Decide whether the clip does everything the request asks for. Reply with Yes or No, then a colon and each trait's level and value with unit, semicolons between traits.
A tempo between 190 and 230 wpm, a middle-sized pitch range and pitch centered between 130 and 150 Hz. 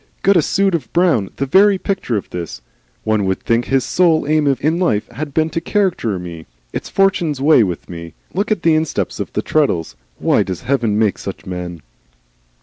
No: average, 195 wpm; wide, 8.8 semitones; medium, 140 Hz